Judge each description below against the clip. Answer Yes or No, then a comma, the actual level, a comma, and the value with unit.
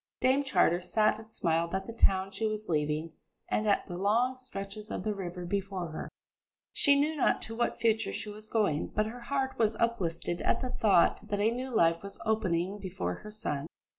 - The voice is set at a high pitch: Yes, high, 210 Hz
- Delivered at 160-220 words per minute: Yes, average, 200 wpm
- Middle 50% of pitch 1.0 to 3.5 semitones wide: No, average, 4.3 semitones